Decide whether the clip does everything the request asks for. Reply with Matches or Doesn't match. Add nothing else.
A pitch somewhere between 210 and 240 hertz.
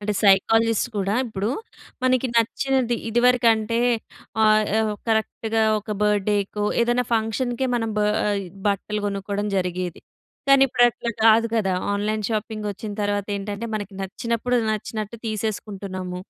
Matches